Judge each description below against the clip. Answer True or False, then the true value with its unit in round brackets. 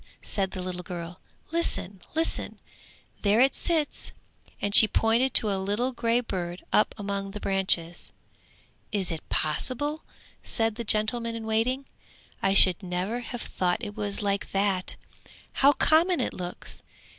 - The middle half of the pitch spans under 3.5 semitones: False (4.1 semitones)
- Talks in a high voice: True (210 Hz)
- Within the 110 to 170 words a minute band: True (145 wpm)